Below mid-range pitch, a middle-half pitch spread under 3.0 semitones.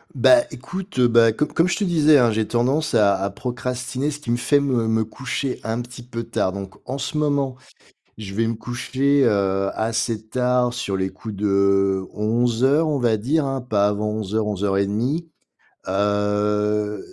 No: low, 115 Hz; average, 4.3 semitones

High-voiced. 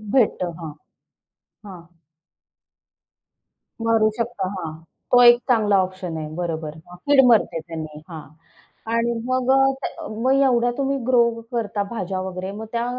Yes: high, 210 Hz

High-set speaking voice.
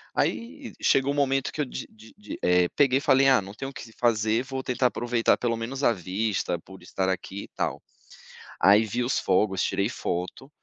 No: low, 115 Hz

